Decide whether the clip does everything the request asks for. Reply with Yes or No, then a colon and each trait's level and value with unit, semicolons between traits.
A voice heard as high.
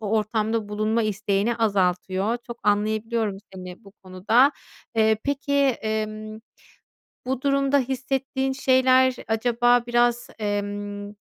Yes: high, 220 Hz